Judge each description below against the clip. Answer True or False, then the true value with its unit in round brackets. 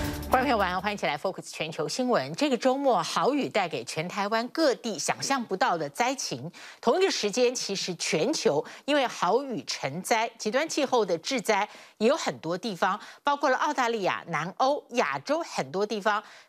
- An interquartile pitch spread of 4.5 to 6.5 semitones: True (5.4 semitones)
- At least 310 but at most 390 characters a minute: False (290 characters per minute)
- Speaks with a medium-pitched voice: False (225 Hz)